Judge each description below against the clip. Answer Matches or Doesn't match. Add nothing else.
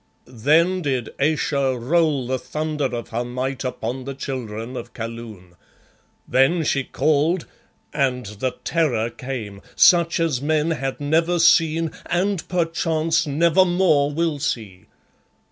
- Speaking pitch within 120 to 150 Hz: Matches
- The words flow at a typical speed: Doesn't match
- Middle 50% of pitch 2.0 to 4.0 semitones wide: Doesn't match